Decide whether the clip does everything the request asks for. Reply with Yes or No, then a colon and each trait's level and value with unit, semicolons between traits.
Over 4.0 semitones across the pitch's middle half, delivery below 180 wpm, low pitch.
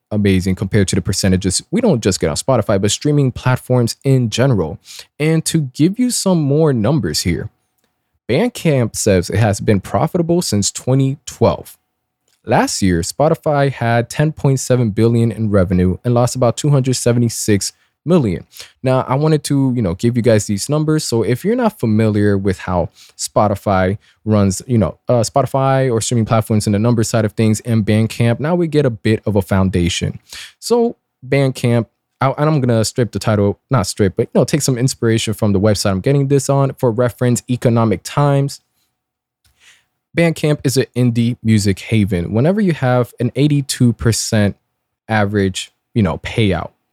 Yes: average, 4.8 semitones; average, 170 wpm; low, 120 Hz